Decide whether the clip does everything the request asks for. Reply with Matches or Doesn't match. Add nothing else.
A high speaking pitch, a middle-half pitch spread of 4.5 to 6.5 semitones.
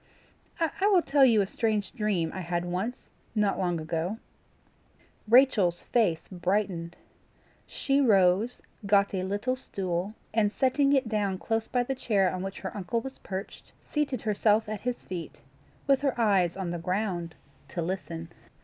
Matches